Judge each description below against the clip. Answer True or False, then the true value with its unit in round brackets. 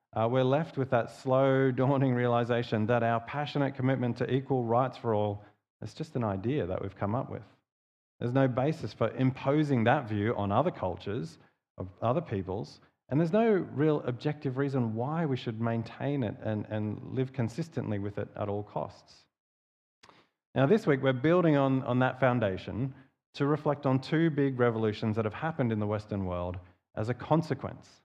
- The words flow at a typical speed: True (180 wpm)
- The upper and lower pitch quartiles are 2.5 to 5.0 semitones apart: True (4.1 semitones)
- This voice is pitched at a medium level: False (125 Hz)